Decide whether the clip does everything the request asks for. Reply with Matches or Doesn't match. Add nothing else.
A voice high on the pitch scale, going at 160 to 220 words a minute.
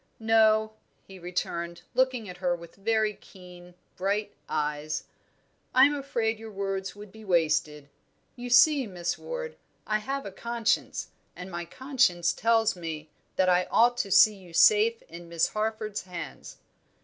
Doesn't match